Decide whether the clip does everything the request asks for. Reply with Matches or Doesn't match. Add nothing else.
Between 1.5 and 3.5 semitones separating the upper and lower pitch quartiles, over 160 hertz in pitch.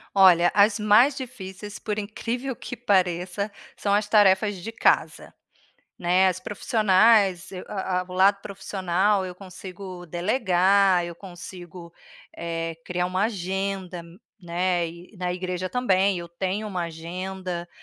Matches